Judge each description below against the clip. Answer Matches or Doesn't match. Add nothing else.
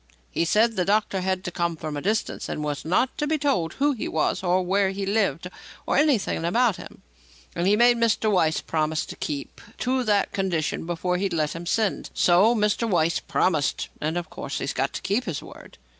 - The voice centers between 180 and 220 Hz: Matches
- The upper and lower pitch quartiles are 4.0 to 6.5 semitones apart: Matches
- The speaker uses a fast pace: Matches